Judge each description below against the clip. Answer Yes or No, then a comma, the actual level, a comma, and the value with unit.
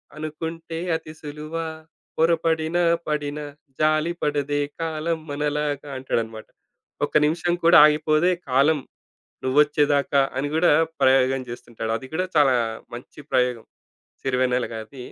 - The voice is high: No, medium, 150 Hz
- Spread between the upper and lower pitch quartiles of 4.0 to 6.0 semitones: No, average, 3.1 semitones